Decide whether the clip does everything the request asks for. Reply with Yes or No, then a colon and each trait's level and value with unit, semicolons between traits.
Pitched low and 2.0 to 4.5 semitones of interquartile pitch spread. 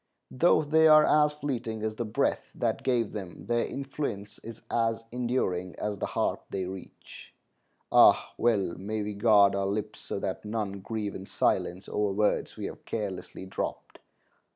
Yes: low, 110 Hz; average, 3.3 semitones